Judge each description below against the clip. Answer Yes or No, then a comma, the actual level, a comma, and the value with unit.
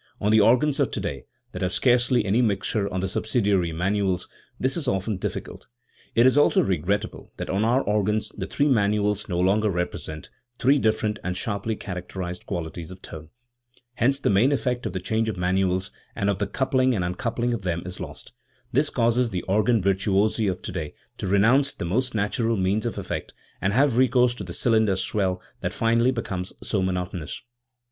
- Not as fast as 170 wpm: No, average, 185 wpm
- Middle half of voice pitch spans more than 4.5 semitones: No, average, 4.1 semitones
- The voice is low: Yes, low, 105 Hz